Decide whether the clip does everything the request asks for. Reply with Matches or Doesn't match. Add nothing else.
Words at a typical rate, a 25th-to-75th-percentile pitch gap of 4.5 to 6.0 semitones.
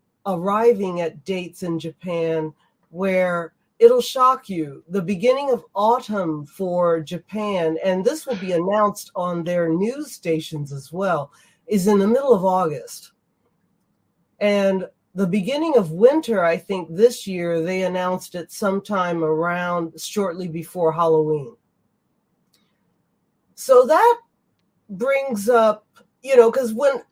Doesn't match